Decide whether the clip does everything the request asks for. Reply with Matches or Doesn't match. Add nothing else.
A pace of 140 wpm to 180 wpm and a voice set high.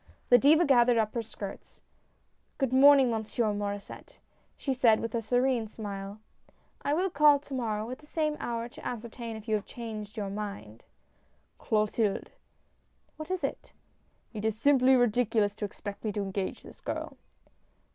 Matches